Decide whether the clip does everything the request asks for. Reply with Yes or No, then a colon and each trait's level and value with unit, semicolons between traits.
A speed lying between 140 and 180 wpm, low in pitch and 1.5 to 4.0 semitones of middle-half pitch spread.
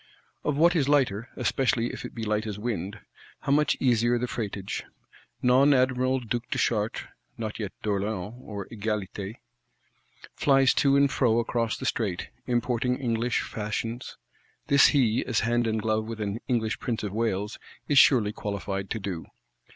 Yes: average, 160 wpm; low, 115 Hz; average, 3.2 semitones